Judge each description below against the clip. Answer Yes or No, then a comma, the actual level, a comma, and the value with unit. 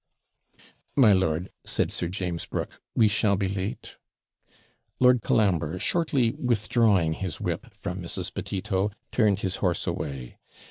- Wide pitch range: No, average, 3.7 semitones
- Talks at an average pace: No, slow, 130 wpm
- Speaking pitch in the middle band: No, very low, 95 Hz